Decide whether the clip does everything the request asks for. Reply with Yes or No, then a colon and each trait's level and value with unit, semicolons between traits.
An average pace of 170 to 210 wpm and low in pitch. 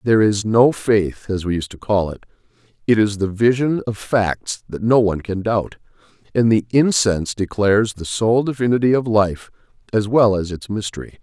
Yes: average, 185 wpm; low, 105 Hz